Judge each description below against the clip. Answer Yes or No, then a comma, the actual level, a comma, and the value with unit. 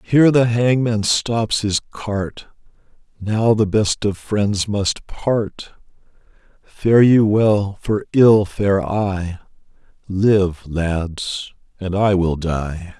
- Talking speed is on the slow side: Yes, slow, 120 wpm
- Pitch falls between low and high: No, low, 100 Hz